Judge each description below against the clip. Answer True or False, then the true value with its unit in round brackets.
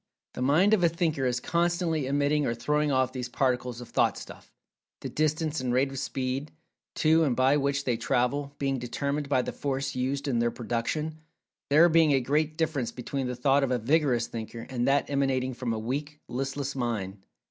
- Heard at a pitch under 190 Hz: True (135 Hz)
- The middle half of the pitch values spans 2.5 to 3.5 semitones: True (3.0 semitones)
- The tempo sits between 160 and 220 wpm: True (195 wpm)